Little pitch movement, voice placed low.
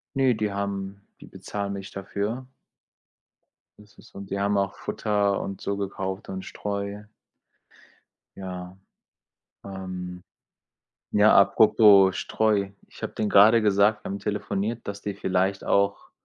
Yes: narrow, 1.3 semitones; low, 100 Hz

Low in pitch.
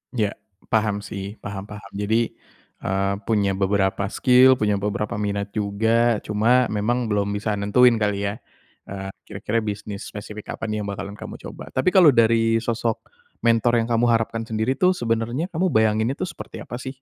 Yes: low, 110 Hz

